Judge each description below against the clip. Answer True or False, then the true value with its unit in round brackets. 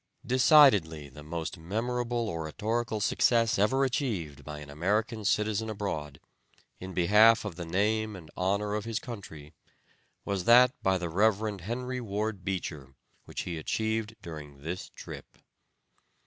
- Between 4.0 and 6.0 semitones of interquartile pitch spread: True (5.2 semitones)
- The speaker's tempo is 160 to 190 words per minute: False (135 wpm)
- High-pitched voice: False (100 Hz)